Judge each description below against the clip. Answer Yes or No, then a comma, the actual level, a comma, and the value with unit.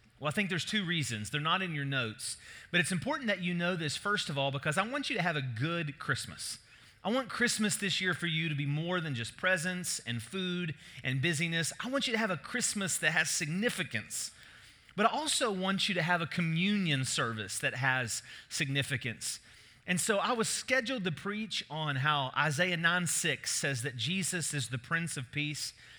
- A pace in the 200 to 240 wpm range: Yes, fast, 205 wpm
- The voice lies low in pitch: No, medium, 170 Hz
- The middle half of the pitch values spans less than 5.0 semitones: No, average, 5.3 semitones